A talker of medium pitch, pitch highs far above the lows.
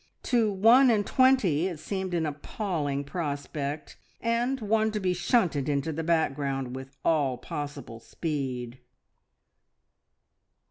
Yes: medium, 160 Hz; wide, 6.7 semitones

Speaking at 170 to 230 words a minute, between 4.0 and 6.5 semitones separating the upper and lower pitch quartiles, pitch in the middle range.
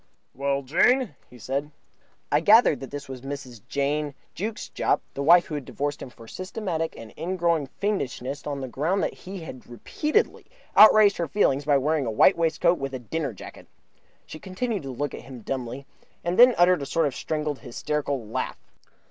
Yes: average, 185 wpm; average, 4.7 semitones; medium, 145 Hz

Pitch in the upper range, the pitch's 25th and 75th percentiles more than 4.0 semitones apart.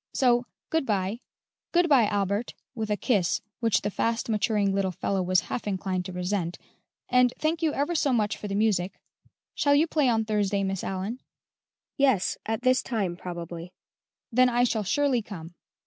Yes: high, 215 Hz; average, 4.6 semitones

